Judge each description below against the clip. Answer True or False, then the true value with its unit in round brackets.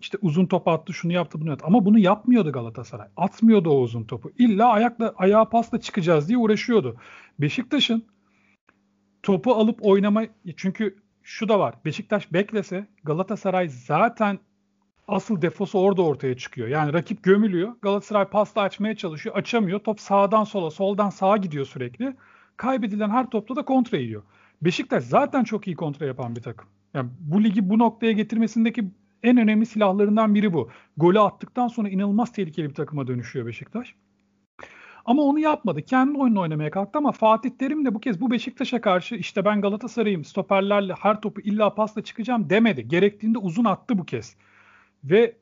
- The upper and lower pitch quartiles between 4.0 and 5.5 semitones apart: True (5.2 semitones)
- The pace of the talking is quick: True (160 wpm)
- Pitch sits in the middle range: False (200 Hz)